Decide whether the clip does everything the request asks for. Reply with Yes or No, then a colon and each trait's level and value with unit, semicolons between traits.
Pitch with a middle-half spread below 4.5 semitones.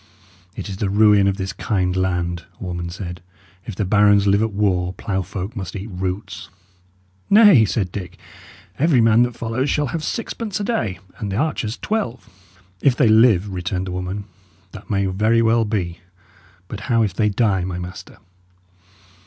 Yes: average, 3.6 semitones